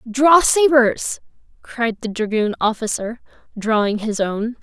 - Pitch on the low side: No, high, 230 Hz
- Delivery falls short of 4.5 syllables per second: Yes, 3.9 syllables/s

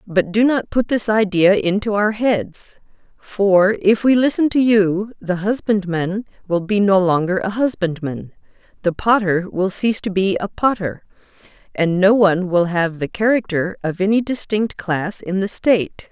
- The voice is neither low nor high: No, high, 200 Hz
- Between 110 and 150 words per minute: No, average, 170 wpm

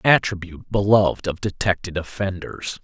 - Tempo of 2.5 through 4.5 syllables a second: No, 5.5 syllables/s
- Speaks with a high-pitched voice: No, very low, 95 Hz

